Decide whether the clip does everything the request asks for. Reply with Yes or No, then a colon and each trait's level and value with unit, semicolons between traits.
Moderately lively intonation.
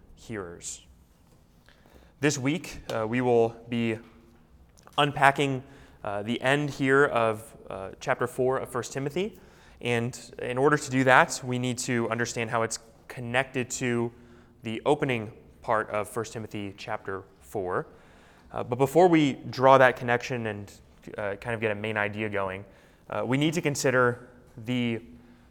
Yes: average, 3.0 semitones